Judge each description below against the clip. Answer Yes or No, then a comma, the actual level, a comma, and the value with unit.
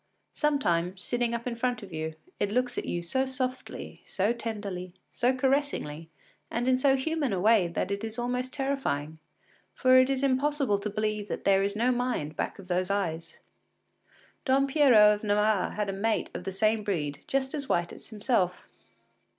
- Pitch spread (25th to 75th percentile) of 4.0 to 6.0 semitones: Yes, average, 5.0 semitones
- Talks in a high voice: Yes, high, 220 Hz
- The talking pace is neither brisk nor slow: Yes, average, 185 wpm